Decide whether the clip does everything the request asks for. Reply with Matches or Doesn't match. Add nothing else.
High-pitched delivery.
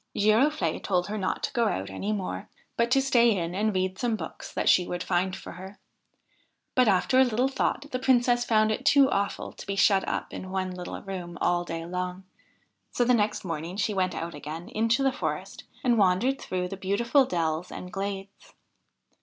Matches